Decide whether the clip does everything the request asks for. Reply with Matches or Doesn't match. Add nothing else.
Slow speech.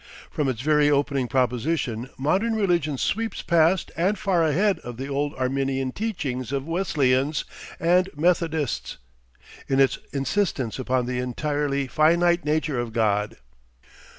Matches